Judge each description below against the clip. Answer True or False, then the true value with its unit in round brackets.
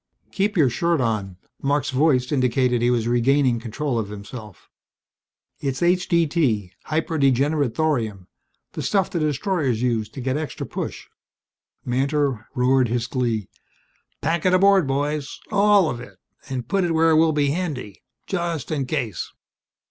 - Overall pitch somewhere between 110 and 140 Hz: True (135 Hz)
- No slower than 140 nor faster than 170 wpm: True (150 wpm)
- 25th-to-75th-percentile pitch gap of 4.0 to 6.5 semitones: True (4.7 semitones)